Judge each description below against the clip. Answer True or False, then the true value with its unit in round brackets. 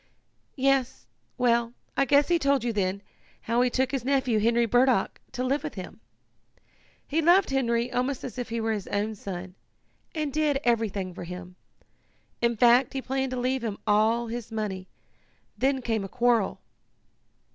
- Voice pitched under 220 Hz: False (235 Hz)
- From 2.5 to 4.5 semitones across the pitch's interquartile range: True (3.5 semitones)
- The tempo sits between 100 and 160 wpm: False (170 wpm)